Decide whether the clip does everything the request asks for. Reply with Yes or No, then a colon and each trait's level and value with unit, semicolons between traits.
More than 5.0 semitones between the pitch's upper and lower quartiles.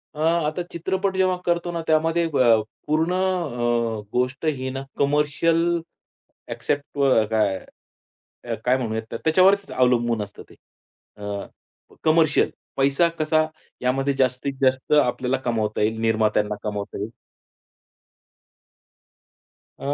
Yes: wide, 5.6 semitones